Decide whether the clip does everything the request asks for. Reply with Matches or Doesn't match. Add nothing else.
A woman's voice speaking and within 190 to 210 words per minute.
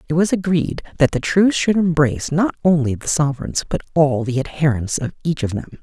Doesn't match